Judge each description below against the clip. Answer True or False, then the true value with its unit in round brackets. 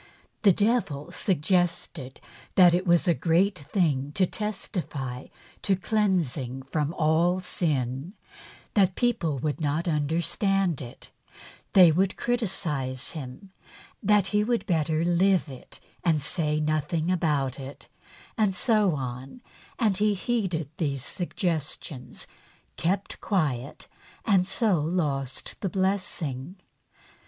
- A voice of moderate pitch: True (170 Hz)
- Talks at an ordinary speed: False (115 wpm)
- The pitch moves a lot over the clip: False (4.9 semitones)